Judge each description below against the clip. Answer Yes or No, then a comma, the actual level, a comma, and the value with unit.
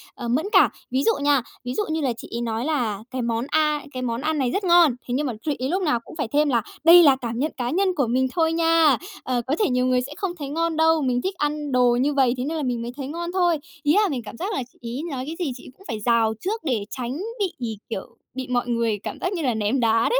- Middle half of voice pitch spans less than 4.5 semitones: No, average, 4.8 semitones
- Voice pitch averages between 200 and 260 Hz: No, very high, 270 Hz